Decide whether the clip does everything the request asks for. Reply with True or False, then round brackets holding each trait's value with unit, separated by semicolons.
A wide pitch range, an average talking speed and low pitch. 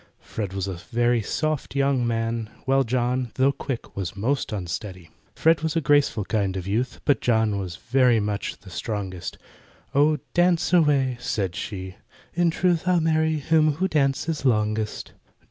True (6.2 semitones; 160 wpm; 125 Hz)